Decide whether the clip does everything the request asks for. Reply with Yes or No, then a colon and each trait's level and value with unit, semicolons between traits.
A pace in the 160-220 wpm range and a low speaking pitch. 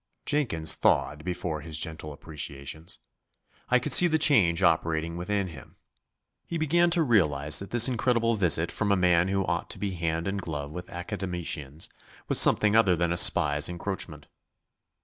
Yes: average, 165 wpm; very low, 90 Hz